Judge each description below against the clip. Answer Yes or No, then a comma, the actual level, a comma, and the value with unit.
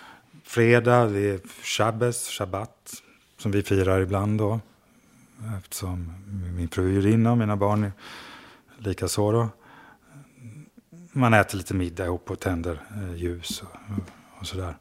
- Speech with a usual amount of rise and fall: Yes, average, 3.7 semitones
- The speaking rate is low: Yes, slow, 120 wpm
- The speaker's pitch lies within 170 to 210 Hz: No, low, 100 Hz